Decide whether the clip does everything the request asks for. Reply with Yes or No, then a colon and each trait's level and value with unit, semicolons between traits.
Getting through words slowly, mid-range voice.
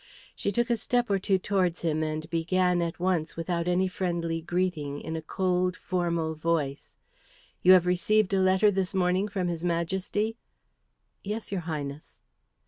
No: average, 160 wpm; medium, 180 Hz